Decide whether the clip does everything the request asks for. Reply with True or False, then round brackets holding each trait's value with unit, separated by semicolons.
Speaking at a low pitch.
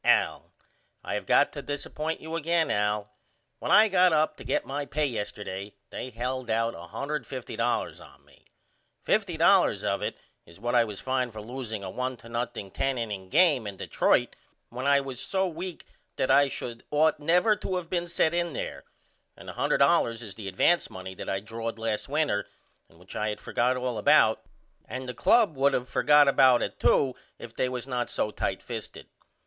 True (125 Hz)